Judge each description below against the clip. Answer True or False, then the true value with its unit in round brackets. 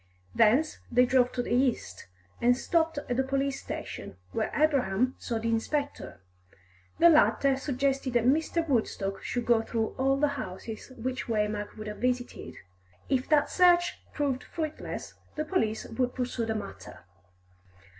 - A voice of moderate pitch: False (255 Hz)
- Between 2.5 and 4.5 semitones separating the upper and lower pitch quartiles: True (3.9 semitones)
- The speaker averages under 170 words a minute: True (150 wpm)